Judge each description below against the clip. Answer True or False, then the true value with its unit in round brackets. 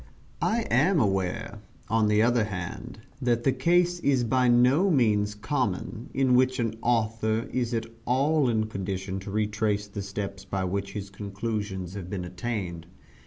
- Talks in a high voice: False (110 Hz)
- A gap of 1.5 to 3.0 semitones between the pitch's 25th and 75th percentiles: False (3.9 semitones)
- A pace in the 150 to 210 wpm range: True (160 wpm)